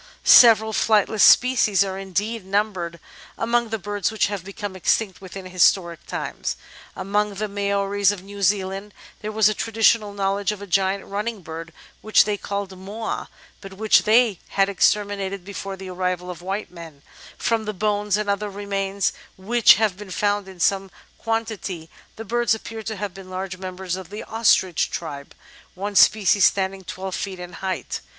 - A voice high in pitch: Yes, high, 200 Hz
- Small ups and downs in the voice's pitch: Yes, narrow, 2.0 semitones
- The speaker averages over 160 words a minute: Yes, average, 170 wpm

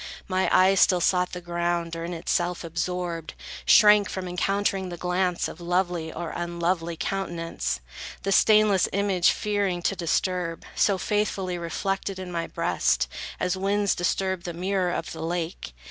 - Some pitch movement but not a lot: No, narrow, 2.1 semitones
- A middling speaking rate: Yes, average, 150 wpm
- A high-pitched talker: No, medium, 180 Hz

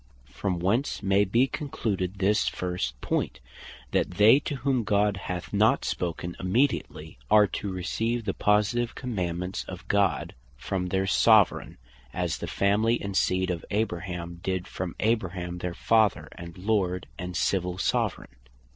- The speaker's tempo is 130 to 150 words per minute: Yes, average, 145 wpm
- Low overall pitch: Yes, very low, 95 Hz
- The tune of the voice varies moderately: Yes, average, 3.2 semitones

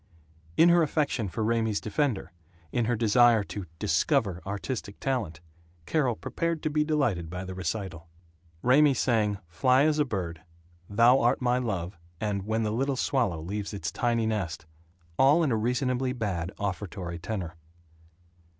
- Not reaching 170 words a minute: Yes, average, 150 wpm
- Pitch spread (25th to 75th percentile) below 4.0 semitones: No, average, 5.2 semitones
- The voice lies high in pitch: No, low, 110 Hz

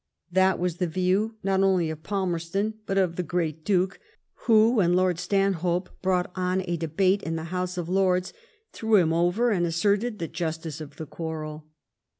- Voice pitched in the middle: Yes, medium, 180 Hz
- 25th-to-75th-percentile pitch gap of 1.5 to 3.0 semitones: Yes, narrow, 2.6 semitones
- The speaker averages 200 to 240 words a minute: No, average, 175 wpm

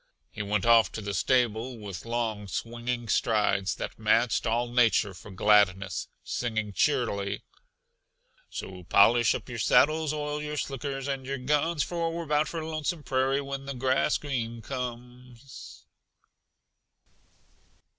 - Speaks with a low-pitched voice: Yes, low, 120 Hz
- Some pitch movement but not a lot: Yes, average, 4.3 semitones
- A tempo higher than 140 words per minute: No, slow, 135 wpm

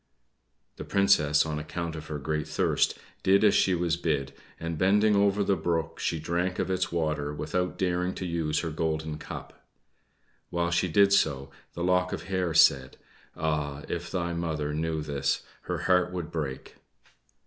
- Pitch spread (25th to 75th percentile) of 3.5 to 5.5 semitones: No, average, 3.0 semitones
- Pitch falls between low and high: No, very low, 85 Hz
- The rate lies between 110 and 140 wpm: No, average, 170 wpm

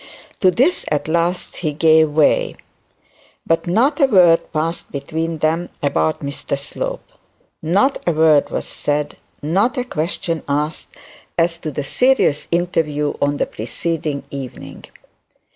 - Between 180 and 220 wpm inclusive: No, slow, 135 wpm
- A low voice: No, medium, 160 Hz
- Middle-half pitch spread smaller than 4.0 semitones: Yes, average, 2.9 semitones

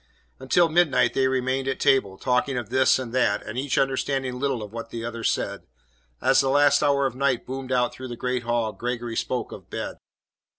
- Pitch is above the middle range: No, low, 130 Hz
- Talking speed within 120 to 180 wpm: No, fast, 205 wpm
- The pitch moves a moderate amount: No, narrow, 2.1 semitones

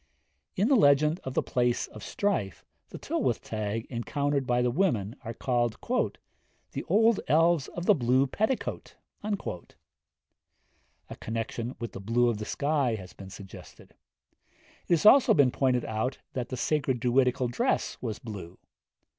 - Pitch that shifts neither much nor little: Yes, average, 5.0 semitones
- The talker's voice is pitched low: Yes, low, 125 Hz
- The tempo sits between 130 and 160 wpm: Yes, average, 155 wpm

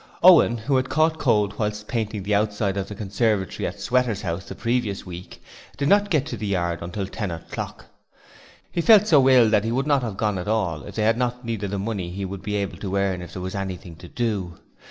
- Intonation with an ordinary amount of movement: Yes, average, 4.0 semitones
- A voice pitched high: No, low, 105 Hz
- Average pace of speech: No, fast, 235 wpm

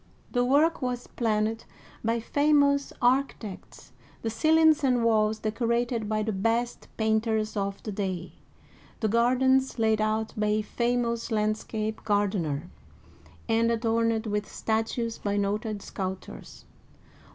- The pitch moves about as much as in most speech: No, narrow, 2.2 semitones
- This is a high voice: Yes, high, 225 Hz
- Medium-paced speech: No, slow, 125 wpm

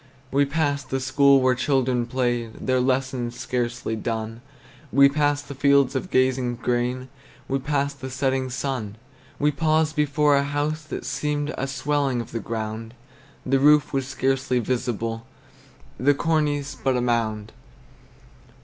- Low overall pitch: Yes, low, 130 Hz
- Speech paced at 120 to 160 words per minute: Yes, average, 145 wpm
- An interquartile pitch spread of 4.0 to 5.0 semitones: No, average, 2.7 semitones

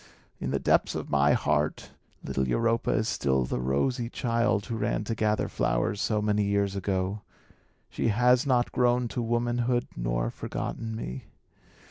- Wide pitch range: Yes, wide, 7.6 semitones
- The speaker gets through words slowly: No, average, 155 wpm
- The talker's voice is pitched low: Yes, low, 105 Hz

